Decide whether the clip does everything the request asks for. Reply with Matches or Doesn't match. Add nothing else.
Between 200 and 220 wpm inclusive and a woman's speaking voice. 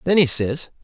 Doesn't match